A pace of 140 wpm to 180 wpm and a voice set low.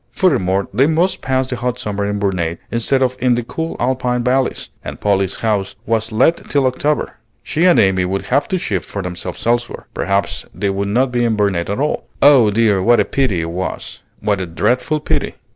No: fast, 205 wpm; low, 115 Hz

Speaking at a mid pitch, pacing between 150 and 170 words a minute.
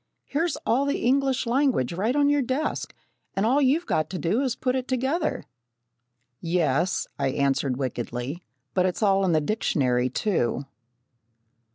No: high, 205 Hz; average, 160 wpm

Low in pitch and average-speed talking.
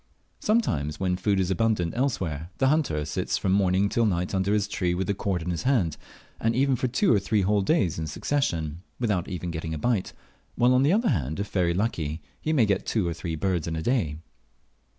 No: very low, 95 Hz; fast, 220 wpm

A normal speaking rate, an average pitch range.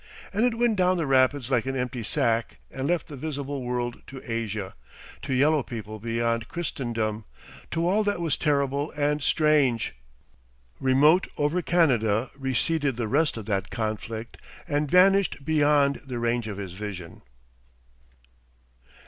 Yes: average, 145 wpm; average, 4.7 semitones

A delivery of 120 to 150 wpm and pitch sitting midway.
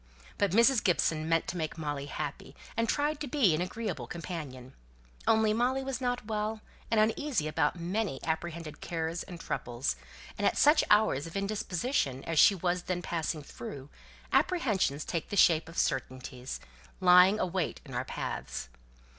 No: average, 165 wpm; medium, 175 Hz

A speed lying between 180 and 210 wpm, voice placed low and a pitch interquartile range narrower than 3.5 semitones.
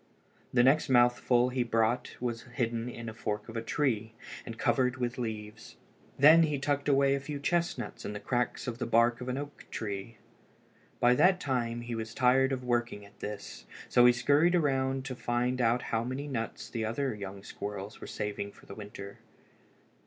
Yes: average, 190 wpm; low, 120 Hz; average, 2.9 semitones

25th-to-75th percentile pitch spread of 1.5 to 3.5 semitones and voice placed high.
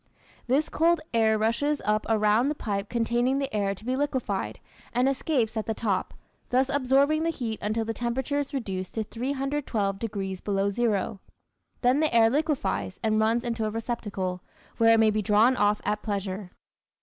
No: average, 4.0 semitones; high, 225 Hz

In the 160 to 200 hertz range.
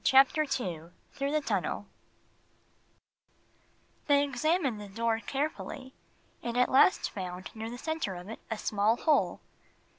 No: high, 245 Hz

